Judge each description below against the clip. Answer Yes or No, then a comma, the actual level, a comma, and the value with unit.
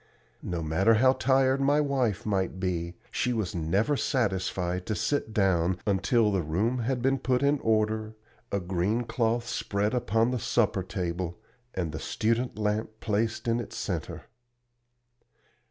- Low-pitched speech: Yes, low, 110 Hz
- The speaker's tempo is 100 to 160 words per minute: Yes, average, 150 wpm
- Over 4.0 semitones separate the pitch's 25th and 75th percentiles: Yes, average, 4.6 semitones